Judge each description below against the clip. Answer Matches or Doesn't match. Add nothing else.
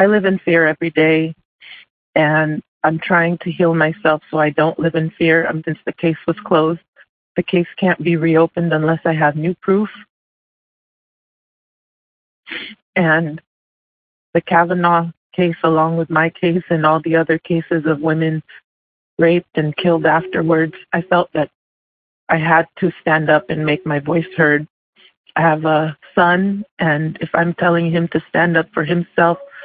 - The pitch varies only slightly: Matches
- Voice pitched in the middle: Matches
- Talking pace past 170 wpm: Doesn't match